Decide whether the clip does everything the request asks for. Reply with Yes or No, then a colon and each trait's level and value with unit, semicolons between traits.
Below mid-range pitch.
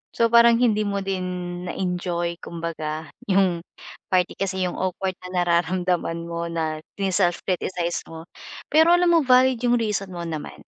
No: medium, 185 Hz